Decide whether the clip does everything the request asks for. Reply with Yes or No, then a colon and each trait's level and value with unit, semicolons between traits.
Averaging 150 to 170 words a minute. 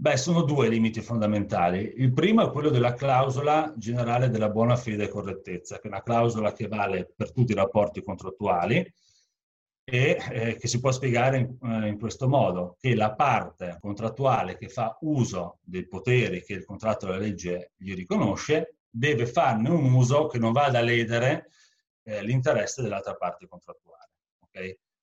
Yes: average, 160 wpm